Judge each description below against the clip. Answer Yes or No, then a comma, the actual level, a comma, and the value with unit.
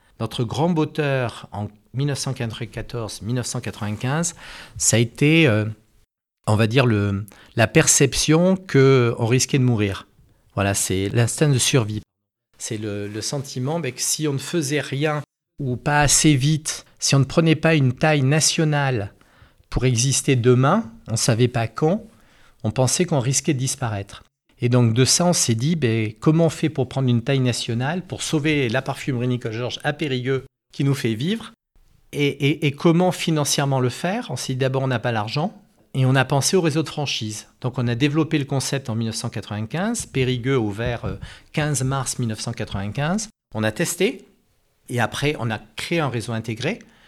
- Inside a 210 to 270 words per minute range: No, average, 175 wpm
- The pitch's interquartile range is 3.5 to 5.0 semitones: Yes, average, 4.7 semitones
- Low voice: Yes, low, 130 Hz